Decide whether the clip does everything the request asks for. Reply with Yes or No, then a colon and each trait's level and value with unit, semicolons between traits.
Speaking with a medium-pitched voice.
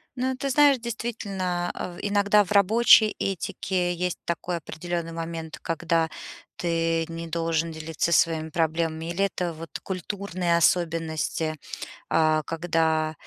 Yes: medium, 170 Hz